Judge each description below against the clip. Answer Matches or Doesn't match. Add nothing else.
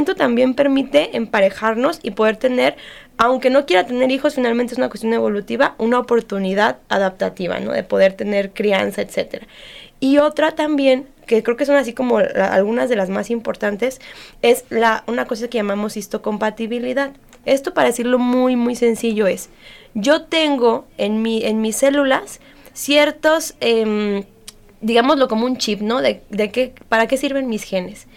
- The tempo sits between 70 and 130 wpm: Doesn't match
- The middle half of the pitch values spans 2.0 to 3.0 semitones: Doesn't match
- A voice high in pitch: Matches